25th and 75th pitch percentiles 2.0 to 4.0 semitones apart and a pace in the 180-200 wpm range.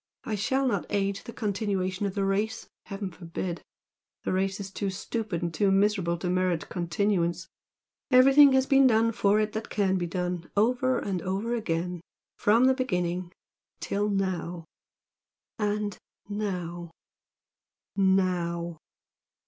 No: average, 3.1 semitones; average, 140 wpm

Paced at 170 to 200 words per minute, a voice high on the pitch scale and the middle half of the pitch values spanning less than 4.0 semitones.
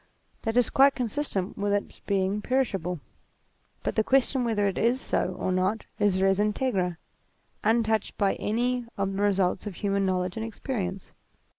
No: average, 160 wpm; high, 205 Hz; average, 3.3 semitones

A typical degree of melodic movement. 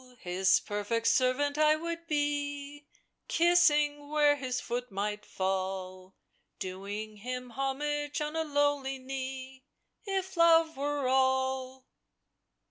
Yes: average, 3.6 semitones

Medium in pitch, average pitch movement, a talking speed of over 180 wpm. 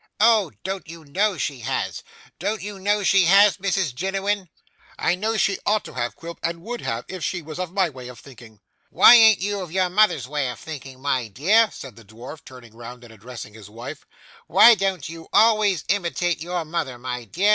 No: medium, 170 Hz; wide, 7.5 semitones; fast, 205 wpm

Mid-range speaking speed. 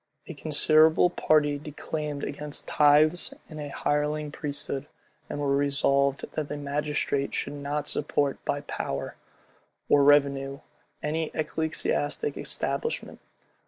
No: slow, 115 wpm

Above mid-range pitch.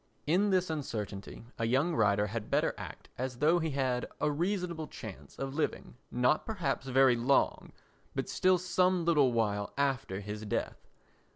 No: low, 135 Hz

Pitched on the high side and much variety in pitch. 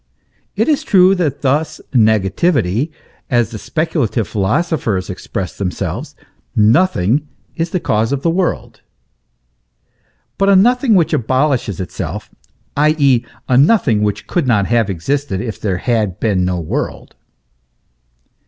No: low, 125 Hz; wide, 7.8 semitones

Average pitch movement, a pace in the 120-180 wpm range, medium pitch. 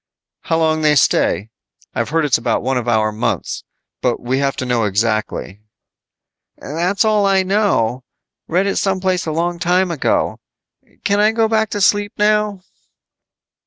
No: wide, 8.1 semitones; average, 160 wpm; medium, 165 Hz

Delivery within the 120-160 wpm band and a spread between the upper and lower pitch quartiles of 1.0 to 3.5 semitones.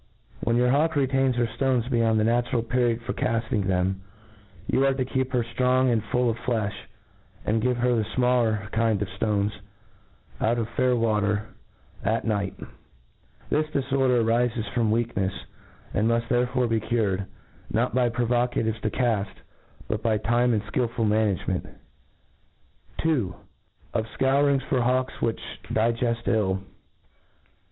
Yes: average, 145 wpm; narrow, 2.4 semitones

